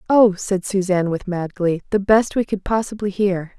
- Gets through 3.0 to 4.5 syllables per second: No, 4.9 syllables/s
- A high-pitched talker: Yes, high, 195 Hz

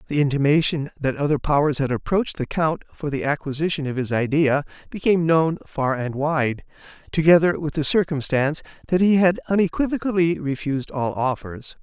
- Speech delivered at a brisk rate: No, average, 155 wpm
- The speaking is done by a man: Yes, male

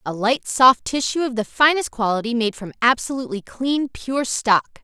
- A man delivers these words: No, female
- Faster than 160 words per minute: Yes, average, 175 wpm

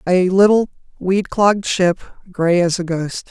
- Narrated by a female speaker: Yes, female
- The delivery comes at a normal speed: Yes, average, 165 wpm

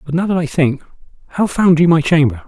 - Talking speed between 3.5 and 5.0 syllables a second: No, 6.1 syllables/s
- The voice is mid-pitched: Yes, medium, 155 Hz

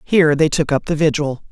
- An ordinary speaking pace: No, fast, 240 wpm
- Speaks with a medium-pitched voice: Yes, medium, 155 Hz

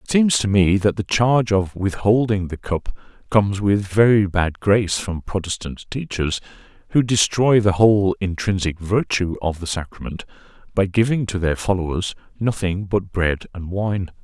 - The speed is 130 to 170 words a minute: Yes, average, 160 wpm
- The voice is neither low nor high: No, low, 100 Hz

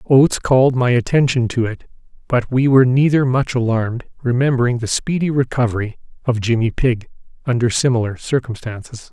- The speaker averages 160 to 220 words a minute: No, average, 145 wpm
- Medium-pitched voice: No, low, 125 Hz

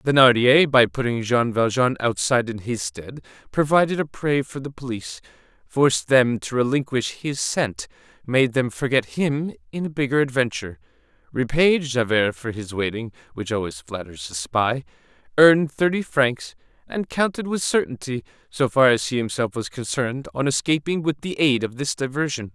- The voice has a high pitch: No, low, 130 Hz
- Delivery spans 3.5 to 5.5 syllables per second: Yes, 5.0 syllables/s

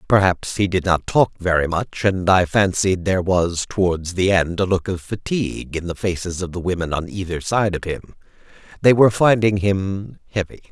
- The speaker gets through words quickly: No, average, 195 wpm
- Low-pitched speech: Yes, very low, 95 Hz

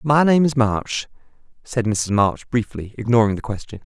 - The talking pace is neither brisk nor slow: Yes, average, 170 wpm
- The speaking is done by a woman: No, male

